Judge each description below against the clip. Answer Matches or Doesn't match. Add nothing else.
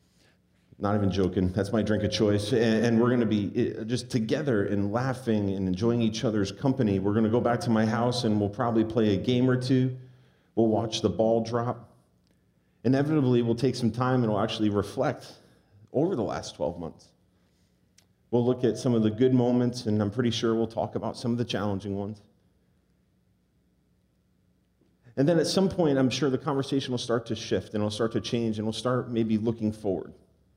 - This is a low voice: Matches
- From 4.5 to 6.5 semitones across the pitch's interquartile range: Doesn't match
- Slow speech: Doesn't match